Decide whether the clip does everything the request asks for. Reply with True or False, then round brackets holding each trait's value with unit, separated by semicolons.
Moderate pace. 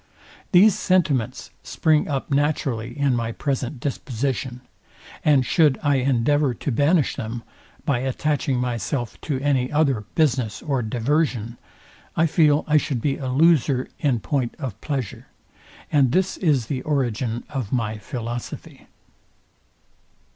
False (130 wpm)